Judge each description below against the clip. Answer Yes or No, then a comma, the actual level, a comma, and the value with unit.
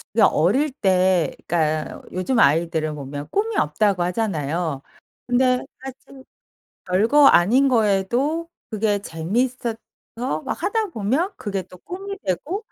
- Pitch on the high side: Yes, high, 205 Hz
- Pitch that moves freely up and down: Yes, wide, 7.4 semitones